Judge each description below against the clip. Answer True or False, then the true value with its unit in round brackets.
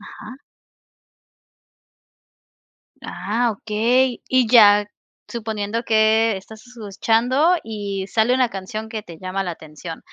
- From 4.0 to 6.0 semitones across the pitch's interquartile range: False (2.7 semitones)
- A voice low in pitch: False (220 Hz)